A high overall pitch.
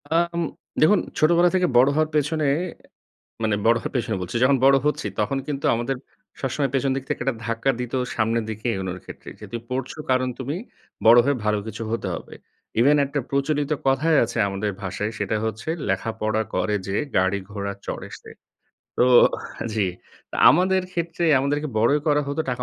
No: low, 130 Hz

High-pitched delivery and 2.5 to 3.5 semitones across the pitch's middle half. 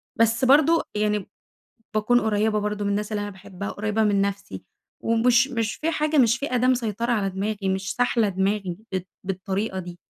Yes: high, 210 Hz; average, 3.1 semitones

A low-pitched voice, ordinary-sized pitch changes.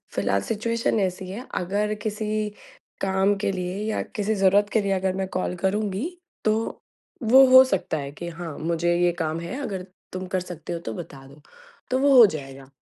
No: high, 190 Hz; average, 3.8 semitones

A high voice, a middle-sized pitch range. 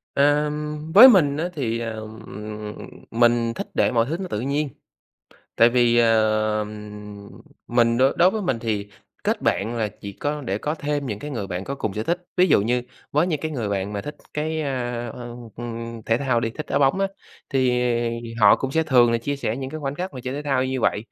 No: low, 125 Hz; average, 4.5 semitones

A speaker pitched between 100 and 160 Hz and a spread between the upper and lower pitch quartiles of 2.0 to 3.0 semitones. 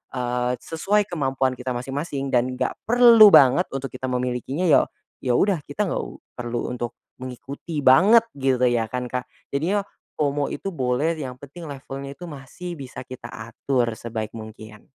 No: low, 135 Hz; average, 4.1 semitones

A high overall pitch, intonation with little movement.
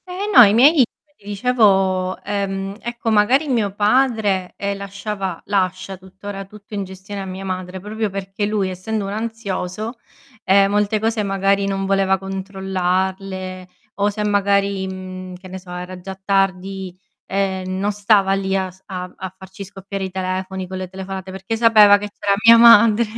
Yes: high, 195 Hz; narrow, 1.6 semitones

